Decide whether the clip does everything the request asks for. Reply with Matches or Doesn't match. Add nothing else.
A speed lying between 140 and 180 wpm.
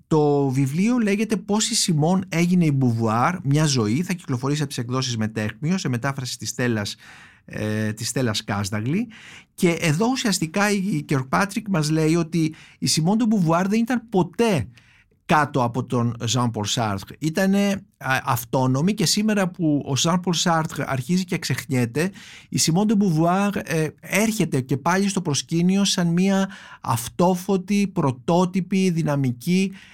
Matches